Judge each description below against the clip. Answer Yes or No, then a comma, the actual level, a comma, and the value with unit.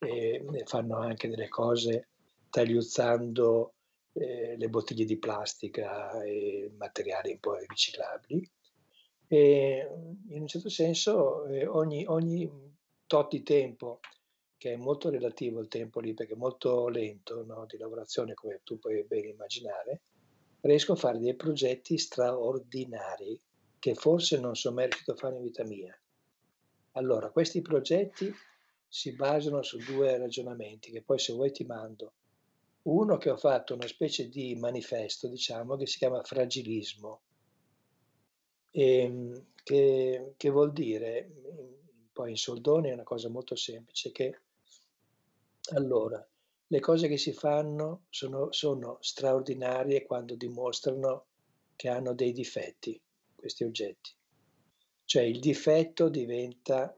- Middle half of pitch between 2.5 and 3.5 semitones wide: No, average, 4.2 semitones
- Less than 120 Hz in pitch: No, low, 130 Hz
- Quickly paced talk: No, average, 130 wpm